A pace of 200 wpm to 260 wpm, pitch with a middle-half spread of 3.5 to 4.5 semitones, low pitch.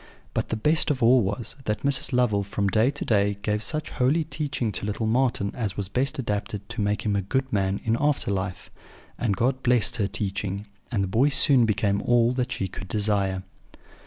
Yes: fast, 205 wpm; average, 4.1 semitones; low, 110 Hz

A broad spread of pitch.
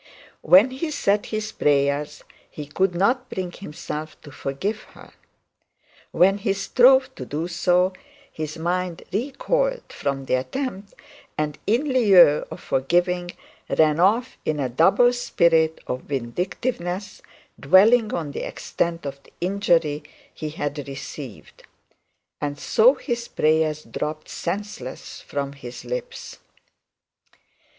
Yes: wide, 6.4 semitones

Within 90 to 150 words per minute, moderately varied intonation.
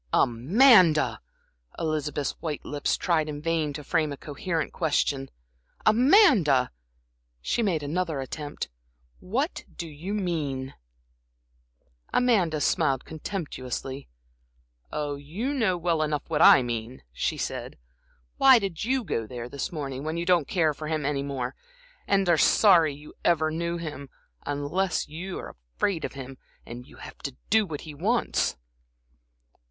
Yes: slow, 135 wpm; average, 4.3 semitones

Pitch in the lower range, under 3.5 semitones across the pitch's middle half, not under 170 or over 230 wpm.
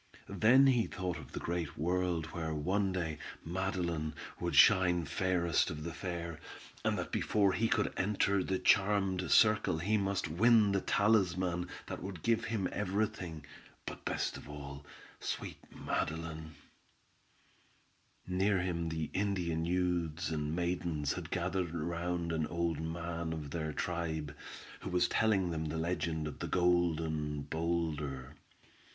No: very low, 85 Hz; average, 2.9 semitones; average, 145 wpm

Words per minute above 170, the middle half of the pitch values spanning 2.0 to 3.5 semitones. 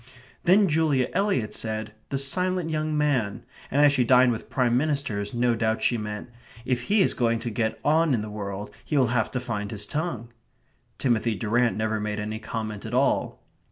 No: average, 190 wpm; average, 4.8 semitones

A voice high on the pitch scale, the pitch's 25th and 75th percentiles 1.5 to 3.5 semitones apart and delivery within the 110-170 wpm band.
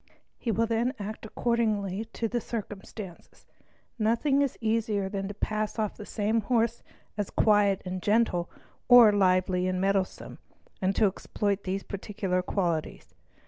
Yes: high, 210 Hz; average, 2.8 semitones; average, 140 wpm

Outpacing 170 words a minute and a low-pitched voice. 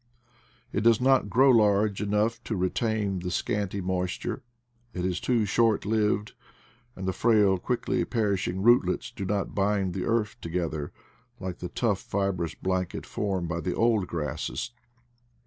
No: average, 145 wpm; low, 100 Hz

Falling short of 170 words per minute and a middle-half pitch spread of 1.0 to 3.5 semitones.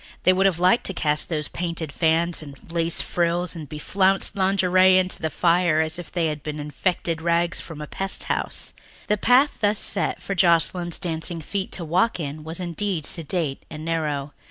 No: average, 185 wpm; average, 2.8 semitones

